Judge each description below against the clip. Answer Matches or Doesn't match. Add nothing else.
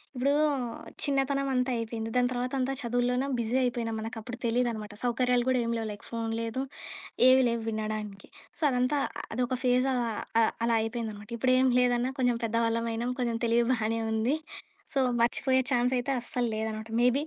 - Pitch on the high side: Matches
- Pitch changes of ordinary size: Doesn't match